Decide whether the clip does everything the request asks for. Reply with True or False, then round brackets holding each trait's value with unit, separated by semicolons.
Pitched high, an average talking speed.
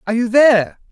True (235 Hz; 195 wpm)